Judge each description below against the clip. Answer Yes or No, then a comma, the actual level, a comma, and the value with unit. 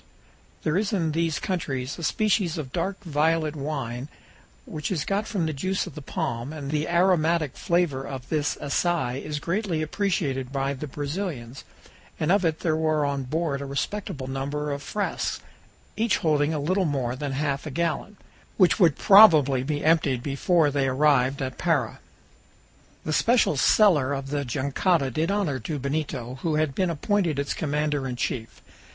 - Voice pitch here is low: No, medium, 150 Hz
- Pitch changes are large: No, average, 3.7 semitones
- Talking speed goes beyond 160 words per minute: Yes, average, 170 wpm